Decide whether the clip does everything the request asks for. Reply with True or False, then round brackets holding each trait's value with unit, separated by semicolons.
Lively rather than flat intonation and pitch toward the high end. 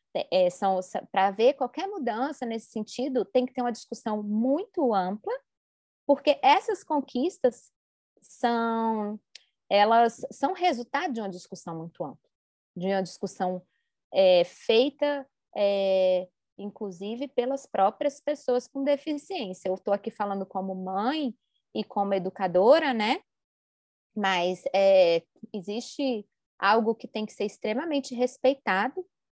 True (5.9 semitones; 225 Hz)